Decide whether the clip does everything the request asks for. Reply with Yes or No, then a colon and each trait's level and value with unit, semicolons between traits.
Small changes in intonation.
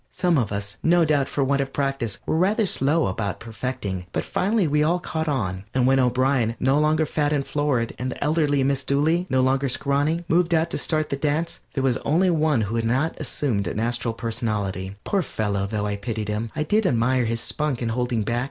No: average, 5.1 semitones